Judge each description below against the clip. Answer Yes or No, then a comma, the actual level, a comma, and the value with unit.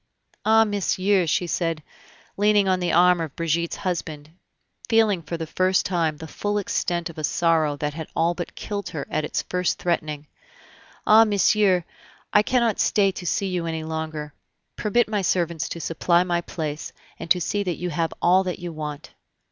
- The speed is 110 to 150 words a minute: No, average, 180 wpm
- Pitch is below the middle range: No, medium, 175 Hz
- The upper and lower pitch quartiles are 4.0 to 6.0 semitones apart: No, average, 3.3 semitones